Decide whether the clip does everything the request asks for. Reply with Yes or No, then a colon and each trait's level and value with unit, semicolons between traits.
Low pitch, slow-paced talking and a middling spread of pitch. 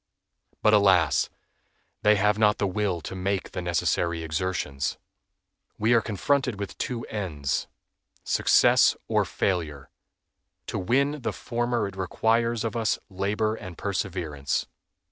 Yes: low, 100 Hz; slow, 125 wpm; average, 4.0 semitones